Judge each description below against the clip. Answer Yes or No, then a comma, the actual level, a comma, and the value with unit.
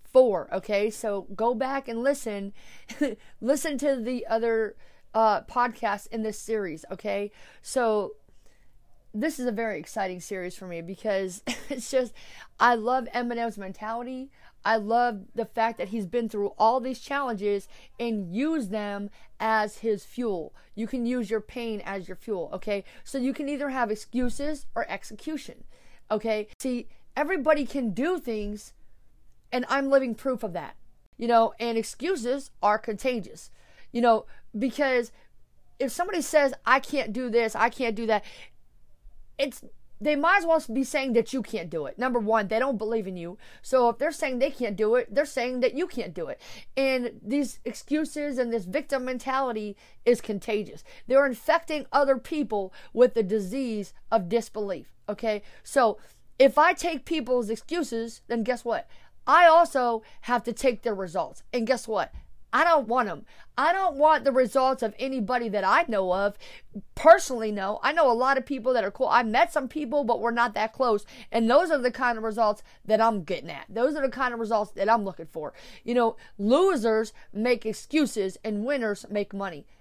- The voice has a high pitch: Yes, high, 235 Hz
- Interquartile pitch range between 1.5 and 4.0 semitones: Yes, average, 3.7 semitones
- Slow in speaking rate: No, average, 175 wpm